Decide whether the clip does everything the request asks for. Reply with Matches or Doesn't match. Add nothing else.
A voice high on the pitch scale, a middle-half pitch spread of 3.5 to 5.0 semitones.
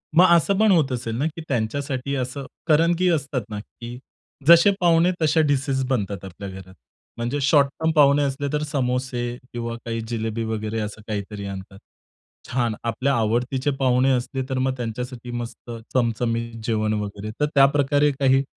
Doesn't match